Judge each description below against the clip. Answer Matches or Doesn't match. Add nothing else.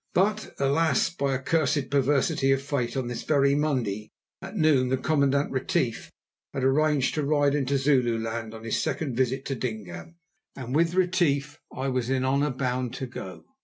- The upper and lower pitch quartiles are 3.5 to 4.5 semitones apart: Doesn't match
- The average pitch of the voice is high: Doesn't match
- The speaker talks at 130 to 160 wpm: Doesn't match